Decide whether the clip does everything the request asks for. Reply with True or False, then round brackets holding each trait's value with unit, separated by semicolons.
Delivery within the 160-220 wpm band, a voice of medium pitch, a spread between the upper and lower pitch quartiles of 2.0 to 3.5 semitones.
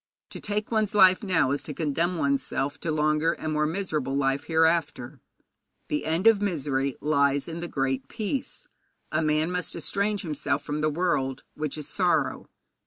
False (175 wpm; 155 Hz; 4.2 semitones)